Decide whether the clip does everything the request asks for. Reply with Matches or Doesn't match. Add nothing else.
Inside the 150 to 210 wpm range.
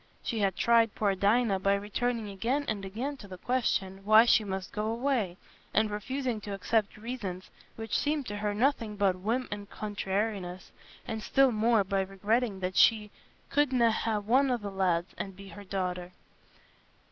Matches